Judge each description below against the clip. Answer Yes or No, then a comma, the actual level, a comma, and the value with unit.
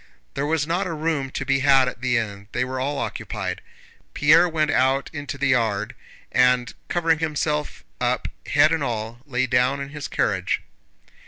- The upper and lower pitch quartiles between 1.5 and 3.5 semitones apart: Yes, average, 3.2 semitones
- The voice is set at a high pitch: No, low, 135 Hz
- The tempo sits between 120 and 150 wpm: No, average, 175 wpm